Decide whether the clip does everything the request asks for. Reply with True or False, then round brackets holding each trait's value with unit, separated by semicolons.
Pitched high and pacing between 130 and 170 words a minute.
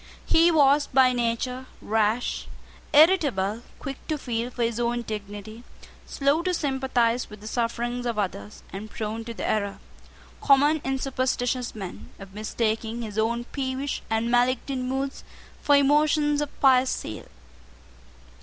True (245 Hz; 140 wpm)